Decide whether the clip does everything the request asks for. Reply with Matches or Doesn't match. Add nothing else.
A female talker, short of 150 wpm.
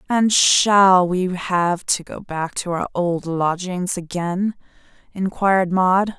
Matches